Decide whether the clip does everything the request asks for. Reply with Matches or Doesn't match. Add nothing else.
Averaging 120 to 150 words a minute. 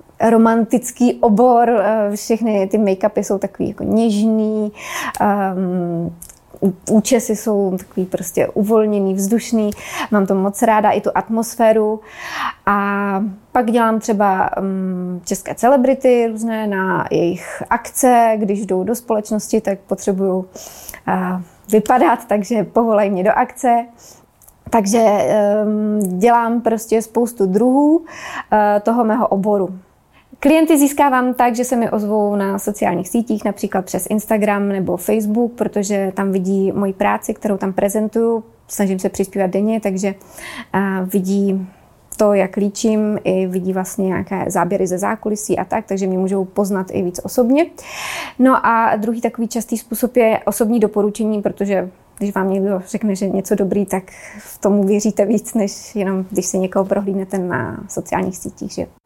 Matches